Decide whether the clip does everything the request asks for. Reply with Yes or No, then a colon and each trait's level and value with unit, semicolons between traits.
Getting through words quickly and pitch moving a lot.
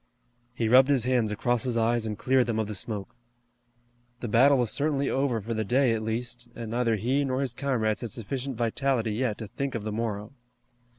No: fast, 210 wpm; average, 2.9 semitones